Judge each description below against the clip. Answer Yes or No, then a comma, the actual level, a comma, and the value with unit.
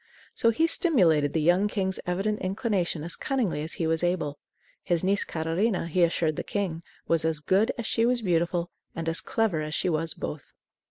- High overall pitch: No, medium, 175 Hz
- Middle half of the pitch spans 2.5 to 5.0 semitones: Yes, average, 4.0 semitones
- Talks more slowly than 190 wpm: No, average, 195 wpm